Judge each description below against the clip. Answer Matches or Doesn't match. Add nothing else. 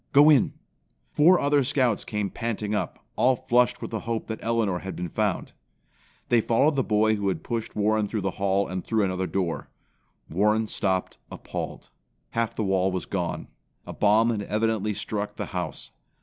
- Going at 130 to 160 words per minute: Doesn't match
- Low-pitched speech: Matches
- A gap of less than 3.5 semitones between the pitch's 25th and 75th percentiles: Matches